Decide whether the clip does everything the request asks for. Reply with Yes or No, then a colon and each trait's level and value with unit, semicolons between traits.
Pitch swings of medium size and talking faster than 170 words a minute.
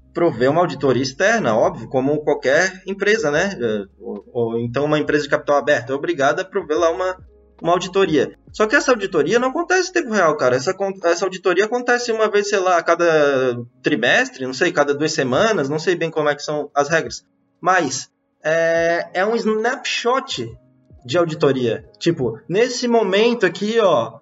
No: wide, 6.1 semitones; average, 180 wpm